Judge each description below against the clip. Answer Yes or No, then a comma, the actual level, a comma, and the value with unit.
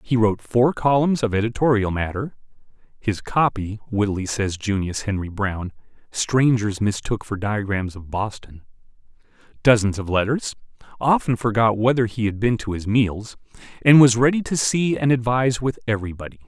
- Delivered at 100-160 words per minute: Yes, average, 150 wpm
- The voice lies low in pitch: Yes, low, 110 Hz